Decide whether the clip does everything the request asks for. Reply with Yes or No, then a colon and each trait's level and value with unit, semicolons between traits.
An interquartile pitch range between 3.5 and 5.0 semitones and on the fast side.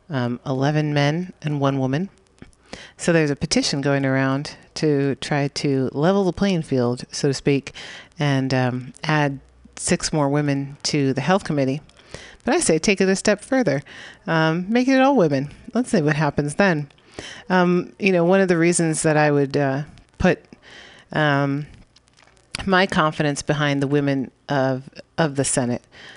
No: average, 4.2 semitones; average, 165 wpm